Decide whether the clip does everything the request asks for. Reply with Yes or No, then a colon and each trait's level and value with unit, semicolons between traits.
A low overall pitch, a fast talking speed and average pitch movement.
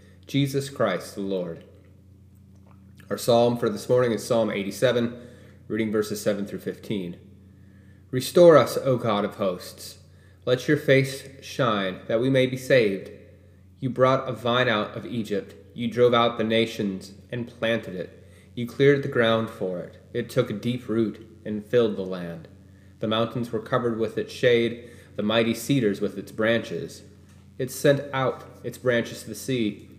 No: low, 110 Hz; average, 165 wpm; average, 3.7 semitones